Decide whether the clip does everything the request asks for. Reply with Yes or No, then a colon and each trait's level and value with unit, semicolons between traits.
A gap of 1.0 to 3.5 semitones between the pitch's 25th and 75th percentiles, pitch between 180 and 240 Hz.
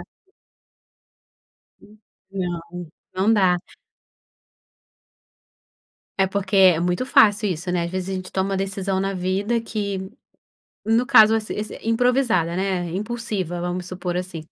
Yes: average, 3.0 semitones; high, 190 Hz